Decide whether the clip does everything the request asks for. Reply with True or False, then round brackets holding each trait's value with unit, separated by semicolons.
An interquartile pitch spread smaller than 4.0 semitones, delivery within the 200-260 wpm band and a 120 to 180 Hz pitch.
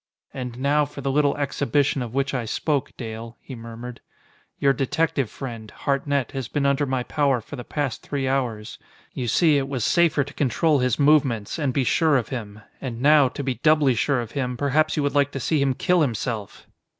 True (2.9 semitones; 205 wpm; 135 Hz)